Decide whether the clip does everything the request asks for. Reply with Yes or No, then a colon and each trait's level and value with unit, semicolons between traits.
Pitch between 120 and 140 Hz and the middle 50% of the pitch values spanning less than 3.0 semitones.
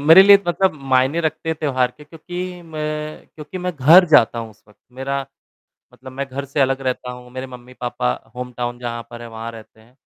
No: low, 135 Hz; average, 4.2 semitones